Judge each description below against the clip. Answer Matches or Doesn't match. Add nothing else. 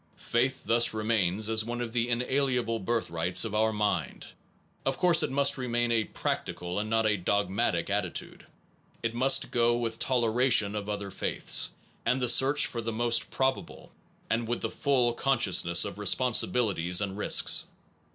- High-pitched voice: Doesn't match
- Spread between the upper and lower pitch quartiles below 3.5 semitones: Matches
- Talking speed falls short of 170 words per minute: Matches